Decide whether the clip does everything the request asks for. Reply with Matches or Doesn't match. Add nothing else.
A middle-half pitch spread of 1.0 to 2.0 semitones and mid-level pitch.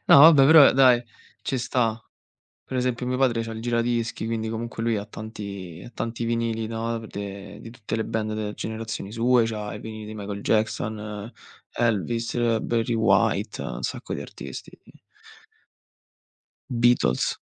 Doesn't match